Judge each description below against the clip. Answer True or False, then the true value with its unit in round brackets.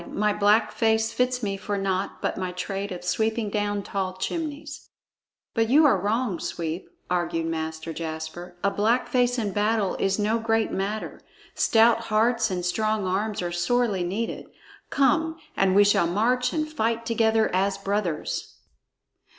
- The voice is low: False (210 Hz)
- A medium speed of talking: True (155 wpm)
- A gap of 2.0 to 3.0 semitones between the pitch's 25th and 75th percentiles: False (3.6 semitones)